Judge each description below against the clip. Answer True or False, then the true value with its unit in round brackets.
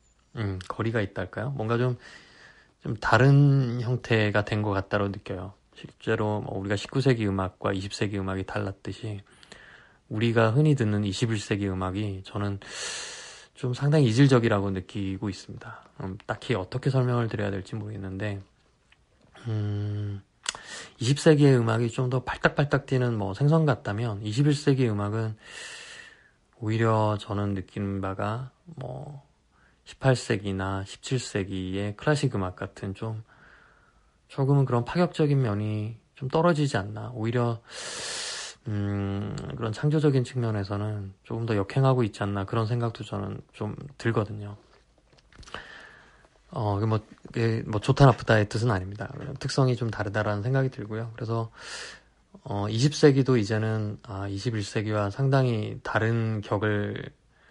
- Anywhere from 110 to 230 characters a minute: False (265 characters per minute)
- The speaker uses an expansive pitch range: False (4.1 semitones)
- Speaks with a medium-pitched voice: False (110 Hz)